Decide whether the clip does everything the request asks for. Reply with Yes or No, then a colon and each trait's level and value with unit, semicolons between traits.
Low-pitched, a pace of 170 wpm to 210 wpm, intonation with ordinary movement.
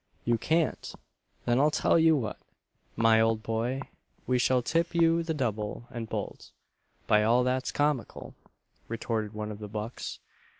No: low, 120 Hz; average, 155 wpm; average, 4.7 semitones